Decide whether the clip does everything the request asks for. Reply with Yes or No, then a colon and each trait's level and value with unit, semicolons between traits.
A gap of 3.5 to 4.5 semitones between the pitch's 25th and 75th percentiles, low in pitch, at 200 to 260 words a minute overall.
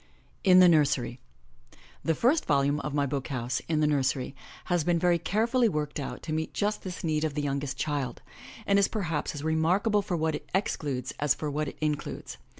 No: average, 3.9 semitones; medium, 155 Hz; fast, 205 wpm